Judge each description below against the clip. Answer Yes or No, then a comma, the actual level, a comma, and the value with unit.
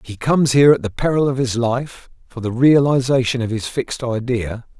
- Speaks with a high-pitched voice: No, low, 125 Hz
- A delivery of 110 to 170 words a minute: No, average, 200 wpm